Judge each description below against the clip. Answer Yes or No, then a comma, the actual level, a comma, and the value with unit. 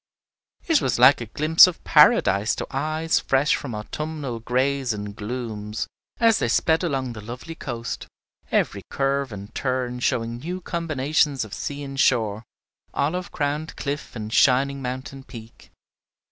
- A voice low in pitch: Yes, low, 130 Hz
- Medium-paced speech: Yes, average, 145 wpm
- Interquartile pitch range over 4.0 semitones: Yes, average, 4.4 semitones